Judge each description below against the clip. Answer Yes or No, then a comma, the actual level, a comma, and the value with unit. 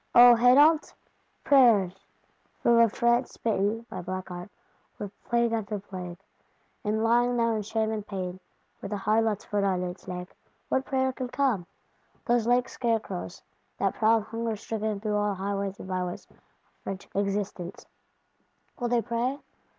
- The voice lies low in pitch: No, high, 220 Hz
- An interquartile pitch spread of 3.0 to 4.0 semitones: Yes, average, 3.3 semitones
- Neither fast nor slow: Yes, average, 150 wpm